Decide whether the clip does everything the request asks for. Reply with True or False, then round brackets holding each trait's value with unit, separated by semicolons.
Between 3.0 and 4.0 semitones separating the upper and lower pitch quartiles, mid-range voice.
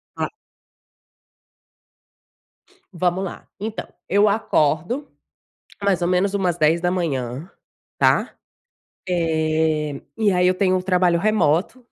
True (3.7 semitones; 180 Hz)